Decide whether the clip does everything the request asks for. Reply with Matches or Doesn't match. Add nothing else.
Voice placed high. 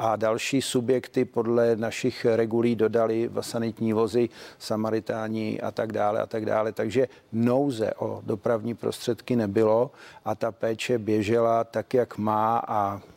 Doesn't match